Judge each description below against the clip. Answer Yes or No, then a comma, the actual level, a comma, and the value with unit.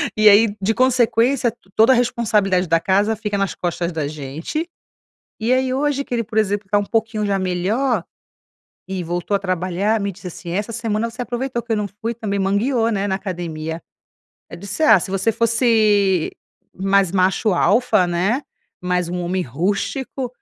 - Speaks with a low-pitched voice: No, high, 205 Hz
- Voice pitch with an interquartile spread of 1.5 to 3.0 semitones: No, average, 4.0 semitones